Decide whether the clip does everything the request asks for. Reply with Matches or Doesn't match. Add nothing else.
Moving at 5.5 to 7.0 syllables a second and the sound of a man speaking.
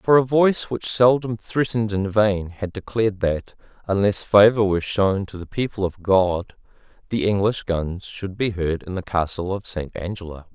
Doesn't match